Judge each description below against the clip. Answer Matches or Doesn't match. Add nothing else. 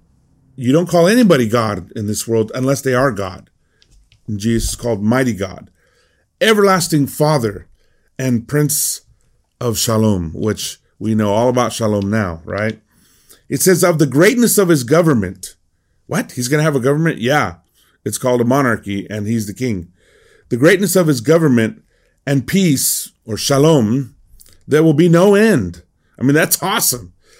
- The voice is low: Matches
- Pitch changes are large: Matches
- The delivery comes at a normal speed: Matches